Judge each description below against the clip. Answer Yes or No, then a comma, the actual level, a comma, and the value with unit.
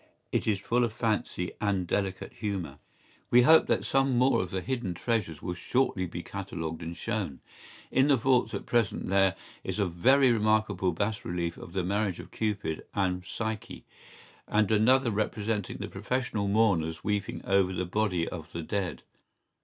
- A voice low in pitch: Yes, low, 100 Hz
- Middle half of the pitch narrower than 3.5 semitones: No, average, 3.8 semitones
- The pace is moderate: Yes, average, 170 wpm